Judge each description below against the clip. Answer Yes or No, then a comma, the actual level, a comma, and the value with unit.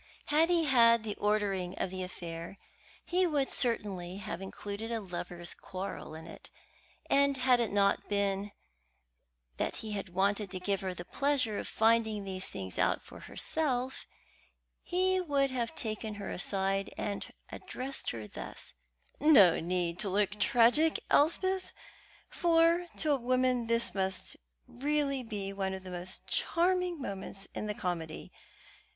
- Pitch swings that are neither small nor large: No, wide, 6.1 semitones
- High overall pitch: Yes, high, 210 Hz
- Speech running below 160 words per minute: Yes, average, 145 wpm